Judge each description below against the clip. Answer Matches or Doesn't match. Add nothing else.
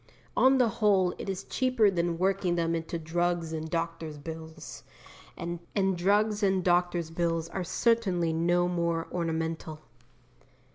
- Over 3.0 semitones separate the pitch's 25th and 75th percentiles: Doesn't match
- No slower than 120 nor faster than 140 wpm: Matches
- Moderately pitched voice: Matches